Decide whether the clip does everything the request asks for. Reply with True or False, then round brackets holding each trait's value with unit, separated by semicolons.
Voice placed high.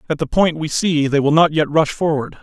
False (155 Hz)